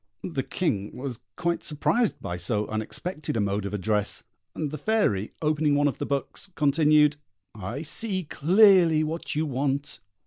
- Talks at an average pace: Yes, average, 160 wpm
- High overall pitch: No, medium, 145 Hz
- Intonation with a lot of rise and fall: Yes, wide, 6.6 semitones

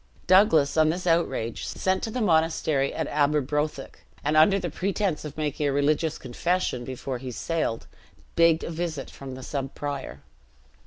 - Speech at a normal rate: Yes, average, 160 wpm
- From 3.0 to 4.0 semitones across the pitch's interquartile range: Yes, average, 3.4 semitones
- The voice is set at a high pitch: No, medium, 155 Hz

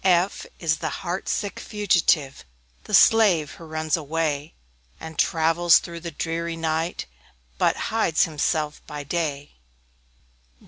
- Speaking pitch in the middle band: Yes, medium, 165 Hz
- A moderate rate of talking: No, slow, 130 wpm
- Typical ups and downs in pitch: No, narrow, 2.0 semitones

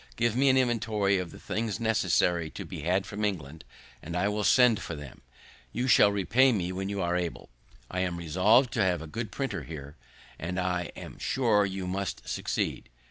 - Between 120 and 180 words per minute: No, average, 195 wpm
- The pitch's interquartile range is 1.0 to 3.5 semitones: No, average, 4.2 semitones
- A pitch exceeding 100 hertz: No, very low, 95 Hz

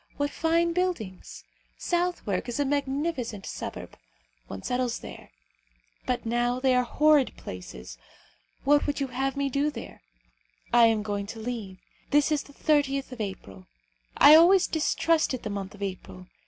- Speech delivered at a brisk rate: No, average, 155 wpm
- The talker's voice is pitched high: Yes, very high, 255 Hz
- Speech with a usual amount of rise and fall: No, wide, 5.7 semitones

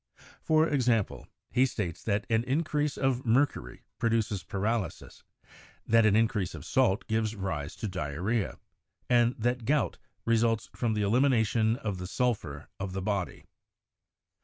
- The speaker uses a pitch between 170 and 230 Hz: No, low, 110 Hz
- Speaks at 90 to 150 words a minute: Yes, average, 145 wpm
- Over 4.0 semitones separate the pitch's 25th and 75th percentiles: No, average, 3.7 semitones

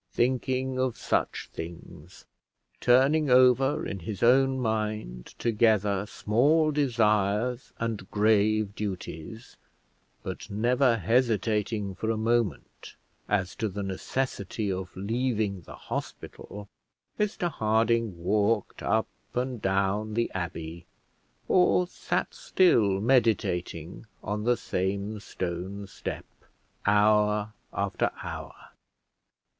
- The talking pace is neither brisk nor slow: No, slow, 100 wpm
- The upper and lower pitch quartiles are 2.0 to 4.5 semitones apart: Yes, average, 3.7 semitones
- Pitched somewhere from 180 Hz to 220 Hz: No, low, 110 Hz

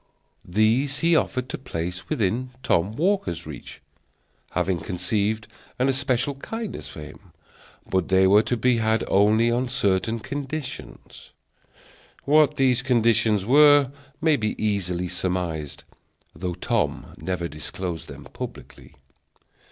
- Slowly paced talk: Yes, slow, 120 wpm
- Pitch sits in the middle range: No, low, 110 Hz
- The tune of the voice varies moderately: No, wide, 6.0 semitones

